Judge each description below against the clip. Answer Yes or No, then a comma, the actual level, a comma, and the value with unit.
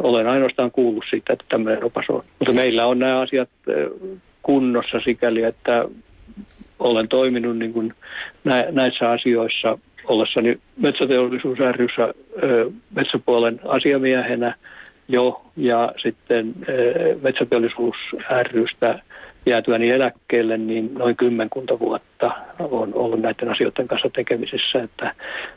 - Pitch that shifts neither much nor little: No, narrow, 1.7 semitones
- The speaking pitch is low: Yes, low, 125 Hz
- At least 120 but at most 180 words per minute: No, average, 100 wpm